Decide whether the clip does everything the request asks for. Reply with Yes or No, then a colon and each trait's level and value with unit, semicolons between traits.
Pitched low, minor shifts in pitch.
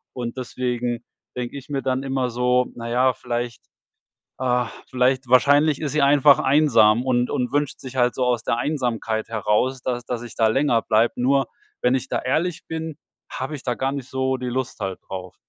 Yes: low, 125 Hz; narrow, 1.9 semitones